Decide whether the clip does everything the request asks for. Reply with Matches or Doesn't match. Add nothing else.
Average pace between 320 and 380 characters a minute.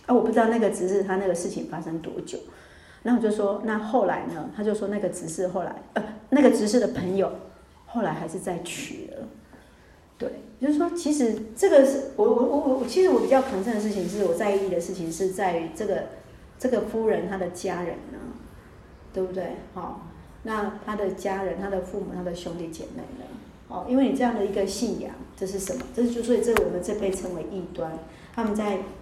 Doesn't match